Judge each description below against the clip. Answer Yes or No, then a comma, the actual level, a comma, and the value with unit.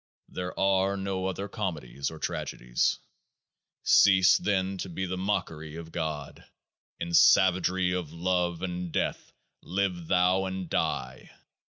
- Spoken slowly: Yes, slow, 130 wpm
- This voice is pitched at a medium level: No, very low, 90 Hz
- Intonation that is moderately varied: No, narrow, 2.2 semitones